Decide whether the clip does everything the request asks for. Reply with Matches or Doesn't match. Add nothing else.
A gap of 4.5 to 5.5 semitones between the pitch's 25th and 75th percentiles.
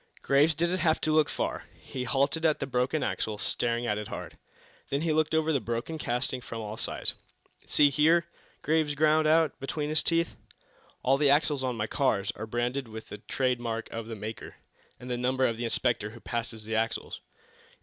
Matches